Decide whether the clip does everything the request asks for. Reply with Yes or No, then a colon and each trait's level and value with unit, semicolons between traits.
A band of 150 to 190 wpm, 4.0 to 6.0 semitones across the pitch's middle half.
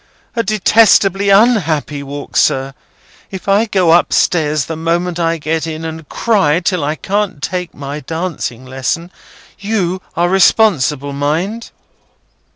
No: slow, 135 wpm; average, 4.7 semitones